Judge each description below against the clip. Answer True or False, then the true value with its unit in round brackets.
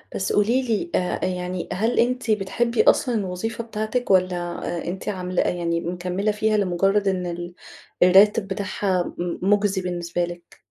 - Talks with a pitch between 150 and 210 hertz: True (190 Hz)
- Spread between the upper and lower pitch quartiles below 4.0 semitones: True (3.1 semitones)